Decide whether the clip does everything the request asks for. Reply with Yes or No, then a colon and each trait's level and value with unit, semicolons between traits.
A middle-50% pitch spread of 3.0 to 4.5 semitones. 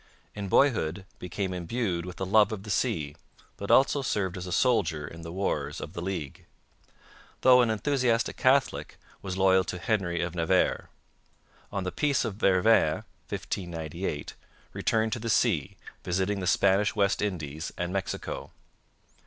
Yes: average, 4.0 semitones